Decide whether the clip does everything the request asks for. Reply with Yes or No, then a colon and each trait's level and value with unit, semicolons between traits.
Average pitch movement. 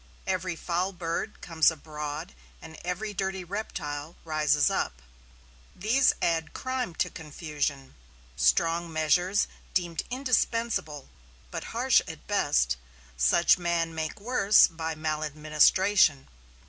Yes: average, 3.8 semitones